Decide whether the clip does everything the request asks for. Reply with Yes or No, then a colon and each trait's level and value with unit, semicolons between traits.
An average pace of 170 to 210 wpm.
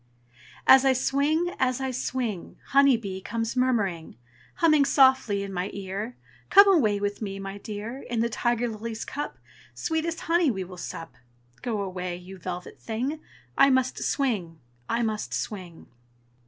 No: average, 155 wpm